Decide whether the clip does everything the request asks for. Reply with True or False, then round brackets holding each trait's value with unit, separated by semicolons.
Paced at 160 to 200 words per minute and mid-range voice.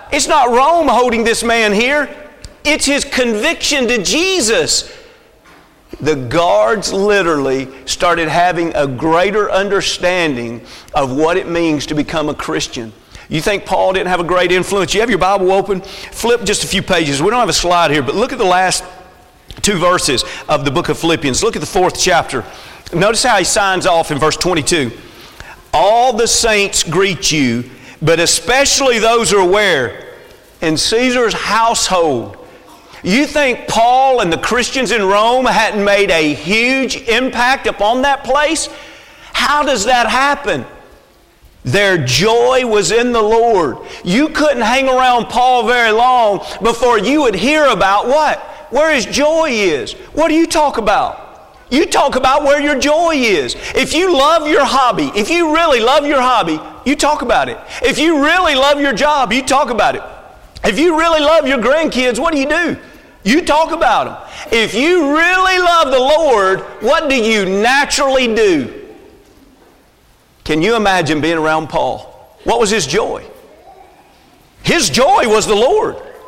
False (165 wpm; 235 Hz)